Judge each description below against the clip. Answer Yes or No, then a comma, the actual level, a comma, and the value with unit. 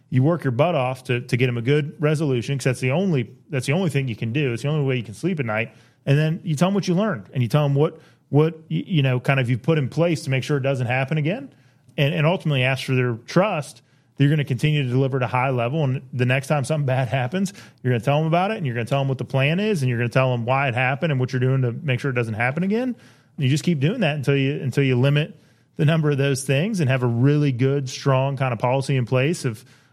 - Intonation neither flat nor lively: Yes, average, 3.0 semitones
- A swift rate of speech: Yes, fast, 305 wpm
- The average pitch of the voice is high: No, medium, 140 Hz